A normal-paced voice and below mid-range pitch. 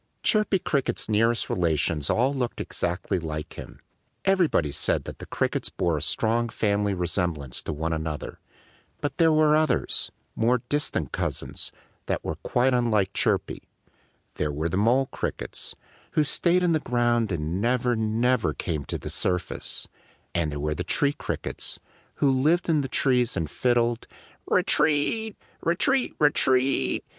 Yes: average, 155 wpm; low, 120 Hz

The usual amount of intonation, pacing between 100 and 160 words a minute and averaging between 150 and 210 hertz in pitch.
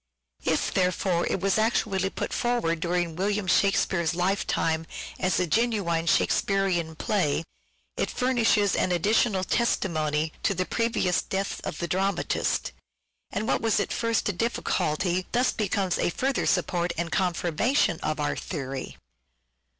Yes: average, 3.5 semitones; average, 140 wpm; medium, 185 Hz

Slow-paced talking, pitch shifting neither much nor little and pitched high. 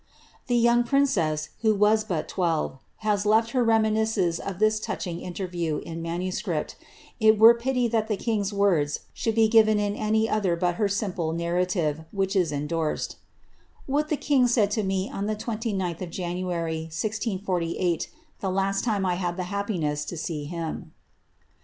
No: average, 155 wpm; average, 4.3 semitones; high, 195 Hz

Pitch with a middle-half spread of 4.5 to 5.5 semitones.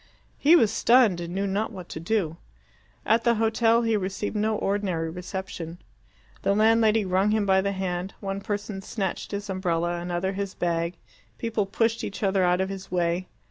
No: average, 3.1 semitones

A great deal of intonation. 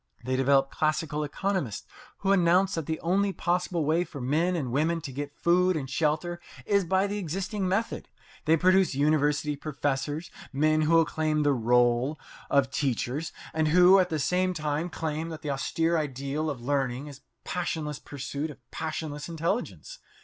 No: average, 3.6 semitones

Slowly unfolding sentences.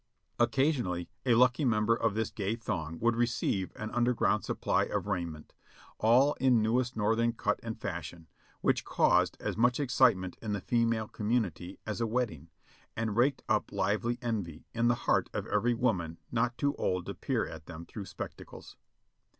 No: average, 175 wpm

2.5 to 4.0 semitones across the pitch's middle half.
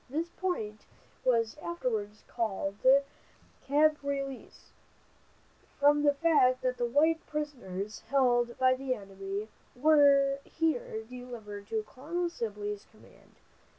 No: average, 5.0 semitones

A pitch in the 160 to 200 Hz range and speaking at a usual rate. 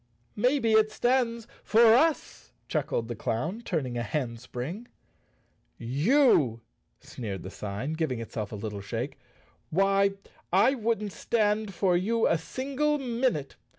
No: high, 190 Hz; slow, 130 wpm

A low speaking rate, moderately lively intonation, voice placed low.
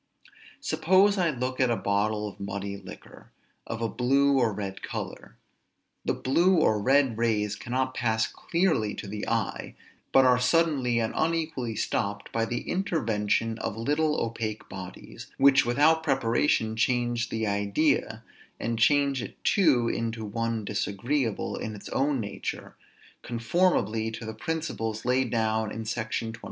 No: average, 145 wpm; average, 4.0 semitones; low, 115 Hz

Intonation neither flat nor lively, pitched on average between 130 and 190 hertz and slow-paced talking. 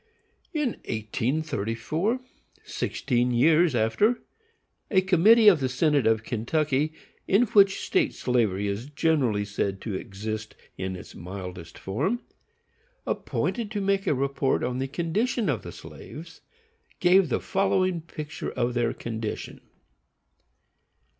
No: wide, 8.9 semitones; medium, 140 Hz; slow, 120 wpm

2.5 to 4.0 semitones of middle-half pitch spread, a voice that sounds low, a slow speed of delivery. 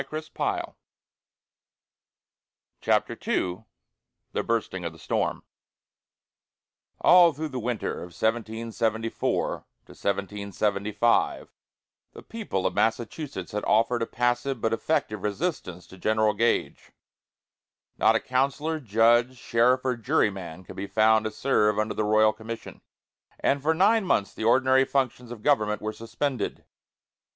Yes: average, 3.6 semitones; low, 115 Hz; slow, 125 wpm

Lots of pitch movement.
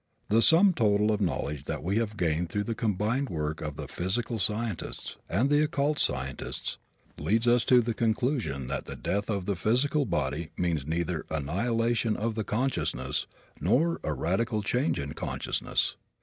Yes: wide, 6.4 semitones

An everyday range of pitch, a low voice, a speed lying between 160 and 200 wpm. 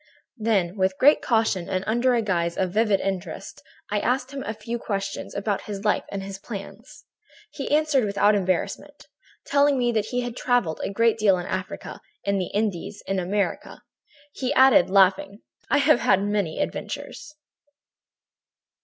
No: average, 3.8 semitones; high, 205 Hz; average, 165 wpm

